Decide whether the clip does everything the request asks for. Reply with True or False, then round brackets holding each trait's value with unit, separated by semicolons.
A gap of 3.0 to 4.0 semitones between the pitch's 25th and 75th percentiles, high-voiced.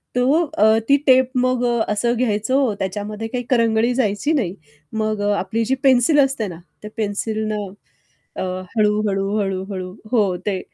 True (3.4 semitones; 220 Hz)